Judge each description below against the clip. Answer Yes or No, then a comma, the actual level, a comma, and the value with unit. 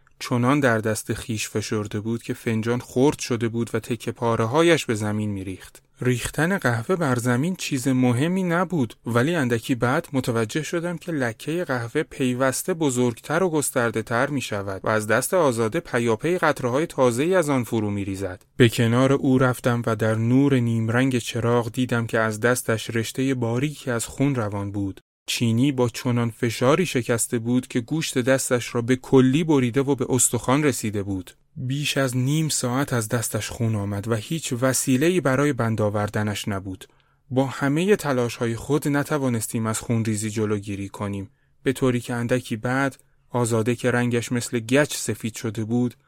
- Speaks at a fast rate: Yes, fast, 170 wpm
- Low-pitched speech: Yes, low, 125 Hz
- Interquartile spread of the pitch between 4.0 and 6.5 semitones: No, average, 3.1 semitones